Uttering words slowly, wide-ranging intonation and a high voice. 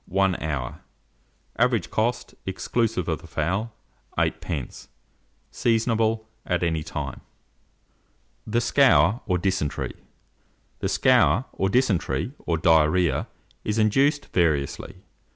No: slow, 100 wpm; wide, 5.7 semitones; very low, 95 Hz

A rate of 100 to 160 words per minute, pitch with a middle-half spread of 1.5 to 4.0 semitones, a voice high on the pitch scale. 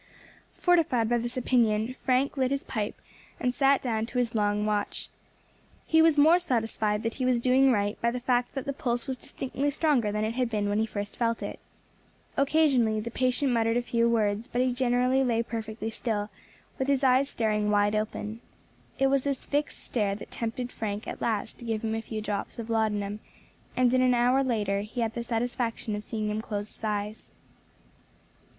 No: average, 200 wpm; average, 3.0 semitones; high, 235 Hz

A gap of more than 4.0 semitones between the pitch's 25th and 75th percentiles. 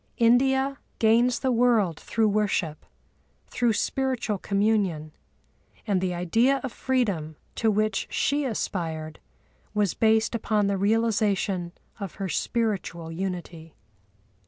Yes: average, 4.4 semitones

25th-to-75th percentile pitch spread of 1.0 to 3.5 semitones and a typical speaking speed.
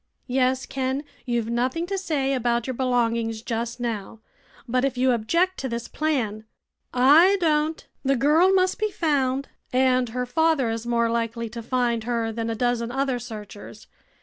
Yes: average, 2.9 semitones; average, 170 wpm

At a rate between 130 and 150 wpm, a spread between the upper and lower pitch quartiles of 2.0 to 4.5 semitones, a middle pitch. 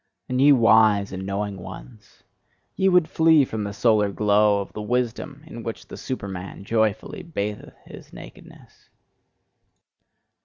No: average, 140 wpm; average, 4.1 semitones; low, 110 Hz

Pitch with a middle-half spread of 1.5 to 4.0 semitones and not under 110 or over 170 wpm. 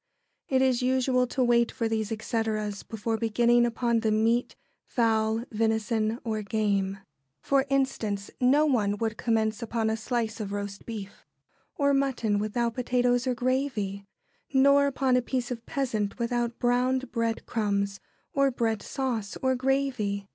Yes: average, 2.8 semitones; average, 145 wpm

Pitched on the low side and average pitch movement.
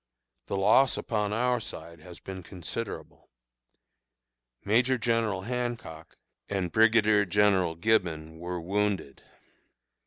Yes: low, 100 Hz; average, 4.4 semitones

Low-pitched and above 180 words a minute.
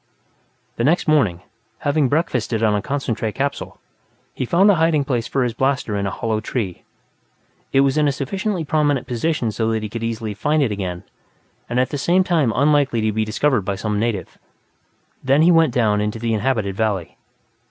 Yes: low, 125 Hz; average, 190 wpm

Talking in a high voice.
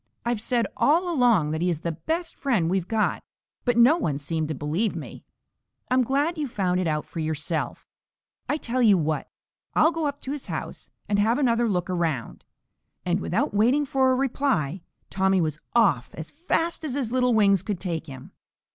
Yes: high, 210 Hz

